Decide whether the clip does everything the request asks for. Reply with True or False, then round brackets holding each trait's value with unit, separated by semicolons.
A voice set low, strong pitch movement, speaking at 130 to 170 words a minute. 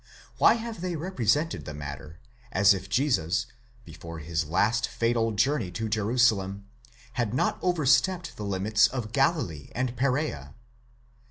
True (110 Hz; 6.3 semitones; 140 wpm)